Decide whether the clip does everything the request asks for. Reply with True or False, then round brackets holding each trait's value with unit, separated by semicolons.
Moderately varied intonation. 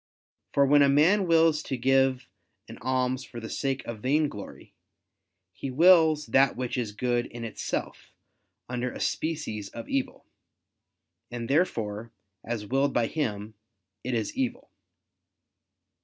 True (4.2 semitones)